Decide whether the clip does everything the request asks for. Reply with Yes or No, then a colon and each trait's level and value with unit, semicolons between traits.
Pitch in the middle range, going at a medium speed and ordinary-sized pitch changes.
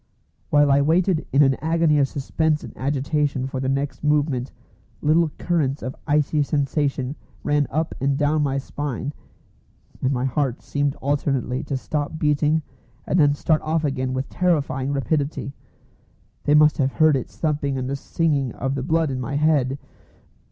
No: medium, 145 Hz; average, 165 wpm; narrow, 2.0 semitones